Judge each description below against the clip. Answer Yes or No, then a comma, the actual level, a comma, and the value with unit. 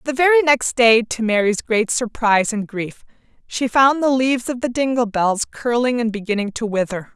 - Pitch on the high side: Yes, high, 235 Hz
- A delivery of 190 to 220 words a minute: Yes, average, 195 wpm